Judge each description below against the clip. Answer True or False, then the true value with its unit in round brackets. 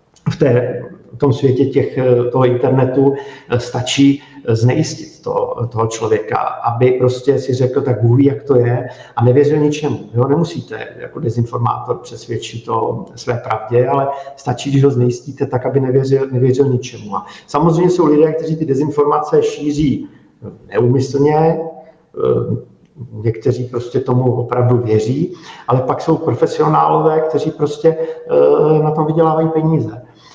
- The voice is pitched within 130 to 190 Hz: True (140 Hz)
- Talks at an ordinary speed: True (130 wpm)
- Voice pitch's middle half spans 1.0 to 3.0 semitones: False (3.9 semitones)